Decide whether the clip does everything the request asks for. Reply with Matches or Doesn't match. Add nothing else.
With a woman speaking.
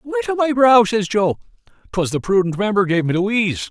Doesn't match